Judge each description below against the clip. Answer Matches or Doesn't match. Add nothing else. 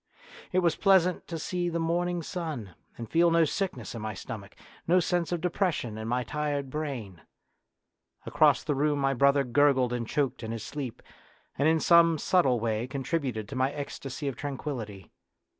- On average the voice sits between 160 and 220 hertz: Doesn't match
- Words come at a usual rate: Matches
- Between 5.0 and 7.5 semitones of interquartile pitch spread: Matches